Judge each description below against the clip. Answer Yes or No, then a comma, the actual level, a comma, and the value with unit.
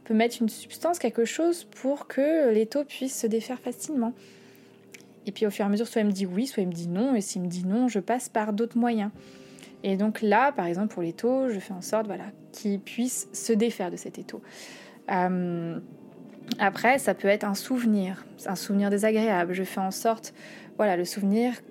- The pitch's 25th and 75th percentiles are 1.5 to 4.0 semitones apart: Yes, average, 3.3 semitones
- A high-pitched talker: Yes, high, 220 Hz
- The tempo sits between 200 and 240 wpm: Yes, fast, 220 wpm